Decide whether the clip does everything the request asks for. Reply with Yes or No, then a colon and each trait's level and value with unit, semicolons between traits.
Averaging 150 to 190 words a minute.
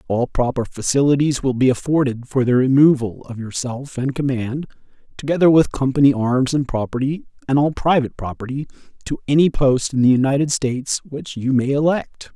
Yes: average, 165 wpm